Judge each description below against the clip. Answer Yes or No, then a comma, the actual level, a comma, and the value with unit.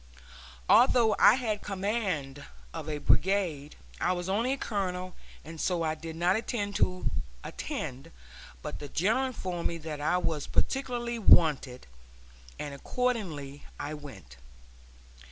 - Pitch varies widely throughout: Yes, wide, 6.1 semitones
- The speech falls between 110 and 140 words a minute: Yes, slow, 135 wpm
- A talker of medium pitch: Yes, medium, 180 Hz